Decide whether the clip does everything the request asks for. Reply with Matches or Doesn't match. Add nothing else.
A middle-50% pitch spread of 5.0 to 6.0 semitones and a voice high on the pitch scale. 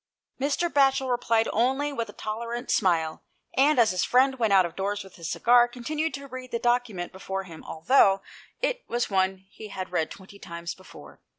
Matches